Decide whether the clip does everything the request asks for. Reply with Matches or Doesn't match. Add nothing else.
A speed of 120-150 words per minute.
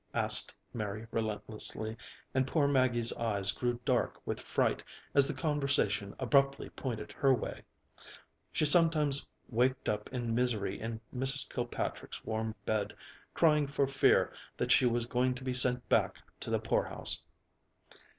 Matches